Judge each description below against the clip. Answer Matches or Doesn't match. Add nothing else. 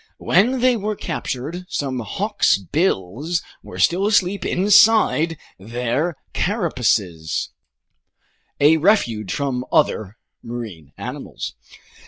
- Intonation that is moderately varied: Doesn't match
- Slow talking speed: Matches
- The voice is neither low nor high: Matches